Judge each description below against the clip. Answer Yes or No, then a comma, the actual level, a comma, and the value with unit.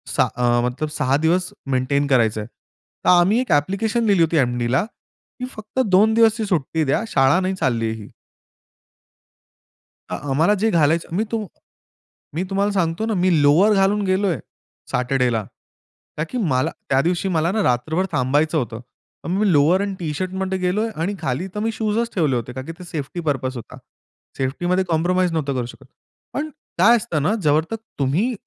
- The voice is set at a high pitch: No, medium, 170 Hz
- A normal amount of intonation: No, wide, 6.3 semitones